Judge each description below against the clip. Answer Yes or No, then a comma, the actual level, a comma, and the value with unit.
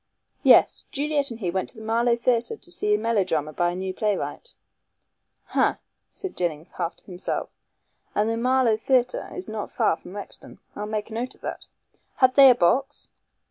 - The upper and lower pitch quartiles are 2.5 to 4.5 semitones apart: No, average, 5.3 semitones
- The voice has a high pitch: Yes, high, 225 Hz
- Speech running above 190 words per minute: No, average, 185 wpm